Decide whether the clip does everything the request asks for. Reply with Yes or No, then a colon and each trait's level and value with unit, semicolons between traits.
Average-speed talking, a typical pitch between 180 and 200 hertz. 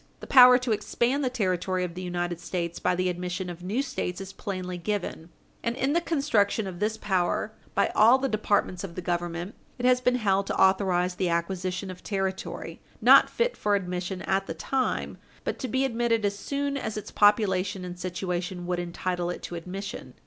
Yes: average, 195 wpm; high, 190 Hz